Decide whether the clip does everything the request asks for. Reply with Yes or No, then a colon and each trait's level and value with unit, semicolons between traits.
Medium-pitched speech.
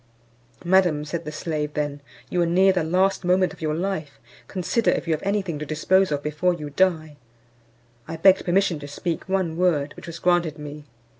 Yes: medium, 170 Hz